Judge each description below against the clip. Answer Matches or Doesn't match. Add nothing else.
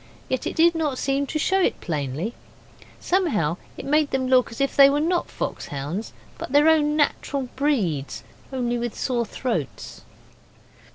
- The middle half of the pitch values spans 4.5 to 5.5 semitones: Matches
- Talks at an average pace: Matches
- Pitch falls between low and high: Doesn't match